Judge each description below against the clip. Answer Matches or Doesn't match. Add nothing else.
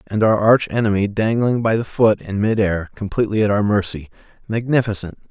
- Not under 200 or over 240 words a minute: Doesn't match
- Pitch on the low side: Matches